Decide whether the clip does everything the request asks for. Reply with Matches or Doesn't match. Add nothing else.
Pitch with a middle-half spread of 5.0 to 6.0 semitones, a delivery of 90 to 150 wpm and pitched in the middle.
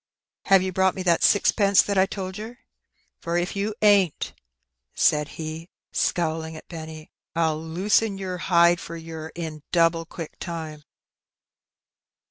Doesn't match